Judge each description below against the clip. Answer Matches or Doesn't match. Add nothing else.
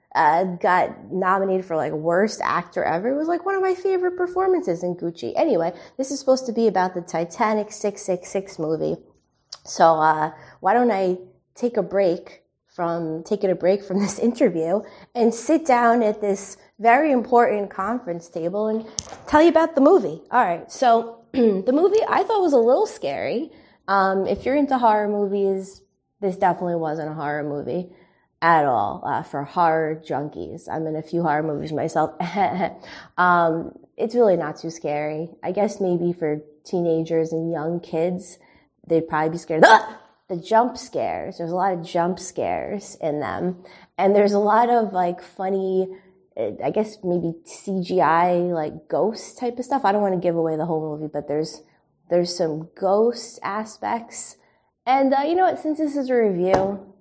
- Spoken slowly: Doesn't match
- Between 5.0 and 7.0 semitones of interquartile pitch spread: Matches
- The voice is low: Doesn't match